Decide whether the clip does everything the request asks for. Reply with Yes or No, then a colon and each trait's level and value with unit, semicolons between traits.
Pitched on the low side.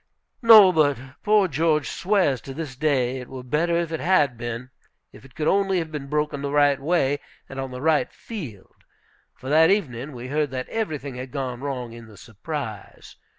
No: medium, 145 Hz